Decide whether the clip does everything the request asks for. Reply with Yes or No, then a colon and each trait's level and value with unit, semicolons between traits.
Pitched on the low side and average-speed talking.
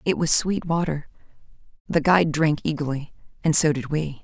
No: medium, 155 Hz; average, 170 wpm